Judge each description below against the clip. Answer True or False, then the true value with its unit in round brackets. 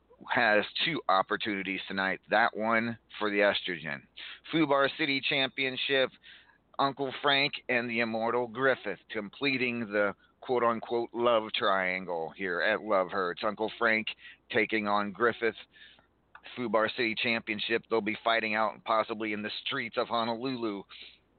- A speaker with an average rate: False (130 wpm)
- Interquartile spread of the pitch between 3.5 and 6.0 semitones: False (2.7 semitones)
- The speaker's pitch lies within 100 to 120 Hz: True (115 Hz)